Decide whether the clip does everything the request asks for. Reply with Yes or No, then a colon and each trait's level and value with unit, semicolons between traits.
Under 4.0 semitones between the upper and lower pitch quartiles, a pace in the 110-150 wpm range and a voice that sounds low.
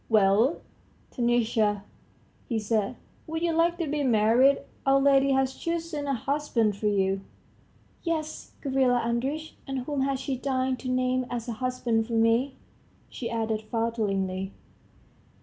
No: average, 3.6 semitones; average, 140 wpm; very high, 255 Hz